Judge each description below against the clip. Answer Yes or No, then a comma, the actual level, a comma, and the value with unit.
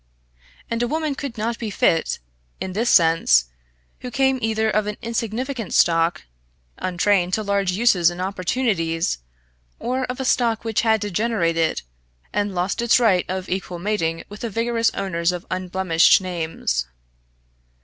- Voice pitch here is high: Yes, high, 200 Hz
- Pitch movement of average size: Yes, average, 4.7 semitones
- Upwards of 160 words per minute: No, average, 150 wpm